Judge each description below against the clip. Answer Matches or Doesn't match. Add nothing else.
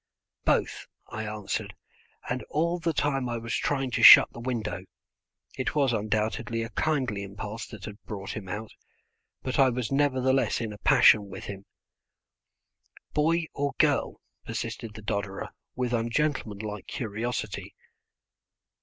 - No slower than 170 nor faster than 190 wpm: Doesn't match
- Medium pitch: Doesn't match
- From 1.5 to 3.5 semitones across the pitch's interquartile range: Doesn't match